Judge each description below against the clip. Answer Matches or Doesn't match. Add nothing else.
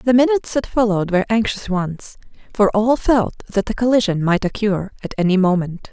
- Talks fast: Doesn't match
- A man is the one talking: Doesn't match